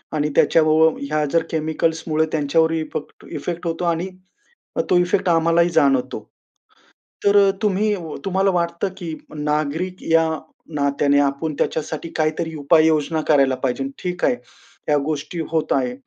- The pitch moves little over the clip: Yes, narrow, 2.3 semitones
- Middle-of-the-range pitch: Yes, medium, 160 Hz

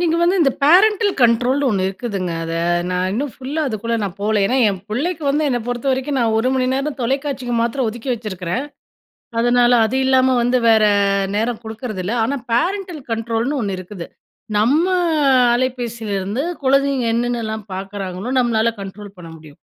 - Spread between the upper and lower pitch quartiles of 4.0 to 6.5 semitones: Yes, average, 4.3 semitones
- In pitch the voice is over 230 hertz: Yes, high, 240 Hz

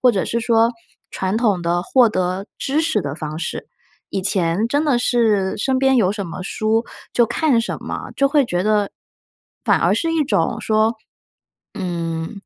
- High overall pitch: Yes, high, 215 Hz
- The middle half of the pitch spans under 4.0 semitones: No, average, 5.0 semitones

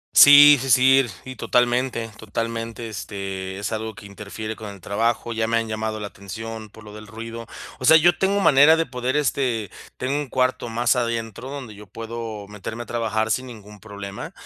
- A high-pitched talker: No, low, 115 Hz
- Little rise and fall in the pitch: No, average, 3.0 semitones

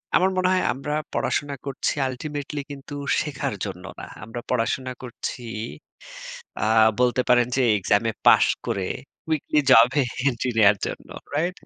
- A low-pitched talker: Yes, low, 130 Hz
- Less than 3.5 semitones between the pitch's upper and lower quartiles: No, average, 4.1 semitones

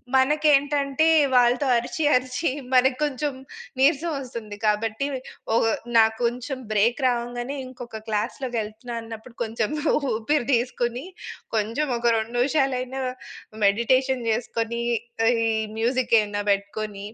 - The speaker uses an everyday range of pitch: Yes, average, 3.1 semitones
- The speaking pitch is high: Yes, high, 245 Hz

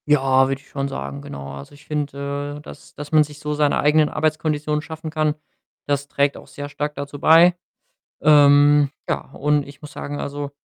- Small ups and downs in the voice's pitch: Yes, narrow, 1.1 semitones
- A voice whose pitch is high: No, medium, 145 Hz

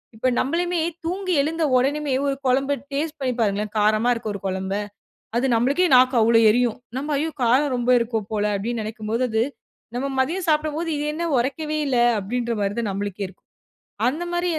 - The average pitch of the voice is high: Yes, very high, 255 Hz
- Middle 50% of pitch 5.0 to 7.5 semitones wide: Yes, wide, 5.4 semitones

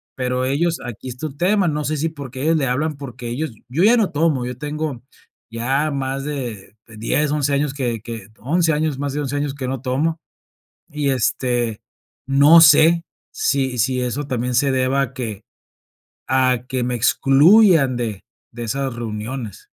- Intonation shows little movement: No, average, 3.2 semitones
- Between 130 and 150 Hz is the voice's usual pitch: Yes, low, 135 Hz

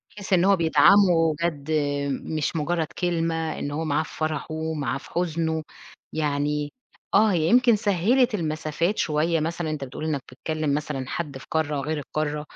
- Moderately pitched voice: Yes, medium, 160 Hz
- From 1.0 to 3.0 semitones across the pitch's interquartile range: Yes, narrow, 2.4 semitones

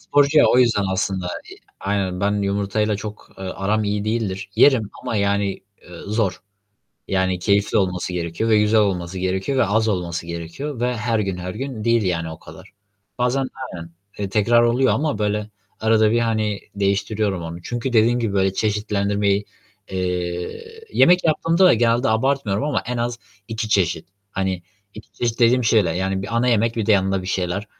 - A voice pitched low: Yes, low, 105 Hz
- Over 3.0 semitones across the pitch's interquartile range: Yes, average, 3.5 semitones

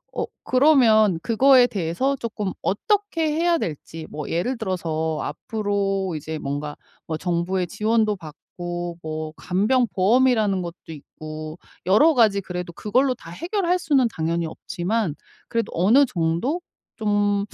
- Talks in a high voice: Yes, high, 200 Hz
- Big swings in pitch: Yes, wide, 6.4 semitones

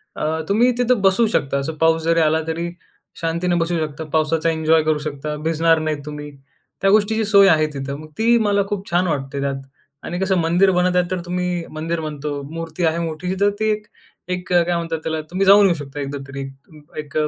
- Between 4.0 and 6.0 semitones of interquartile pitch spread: No, average, 3.0 semitones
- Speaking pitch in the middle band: Yes, medium, 165 Hz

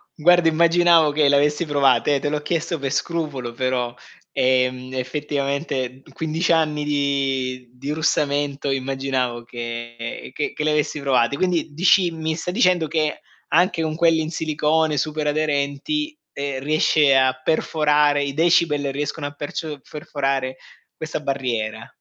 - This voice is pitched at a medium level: Yes, medium, 145 Hz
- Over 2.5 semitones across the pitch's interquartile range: Yes, average, 2.9 semitones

